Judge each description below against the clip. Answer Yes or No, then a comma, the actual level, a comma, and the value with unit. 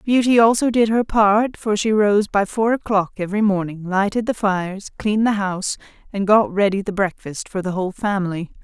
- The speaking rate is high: No, average, 195 wpm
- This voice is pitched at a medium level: No, high, 205 Hz